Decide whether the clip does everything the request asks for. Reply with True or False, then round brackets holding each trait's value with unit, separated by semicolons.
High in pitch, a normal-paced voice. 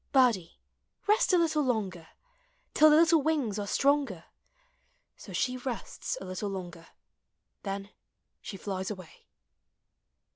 False (220 Hz; 120 wpm)